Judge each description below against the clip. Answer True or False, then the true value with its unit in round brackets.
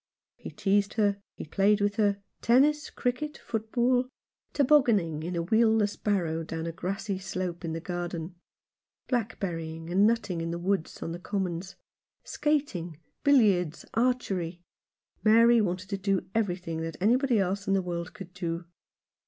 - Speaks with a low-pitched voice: False (195 Hz)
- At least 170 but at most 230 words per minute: False (160 wpm)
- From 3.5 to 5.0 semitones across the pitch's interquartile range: True (4.4 semitones)